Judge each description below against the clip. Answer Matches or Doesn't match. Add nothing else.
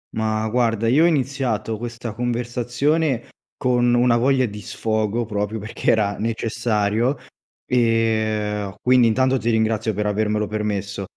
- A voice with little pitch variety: Matches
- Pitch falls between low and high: Doesn't match